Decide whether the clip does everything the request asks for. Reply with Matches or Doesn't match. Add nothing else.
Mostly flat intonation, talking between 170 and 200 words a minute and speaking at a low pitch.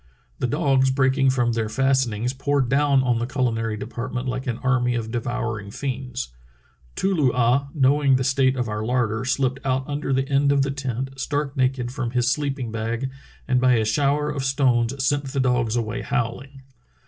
Matches